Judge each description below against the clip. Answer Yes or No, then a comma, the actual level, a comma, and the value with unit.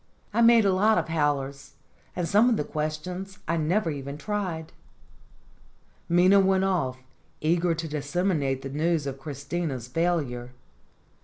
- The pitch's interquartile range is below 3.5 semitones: No, average, 4.6 semitones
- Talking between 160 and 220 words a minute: No, average, 140 wpm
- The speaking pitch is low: No, medium, 165 Hz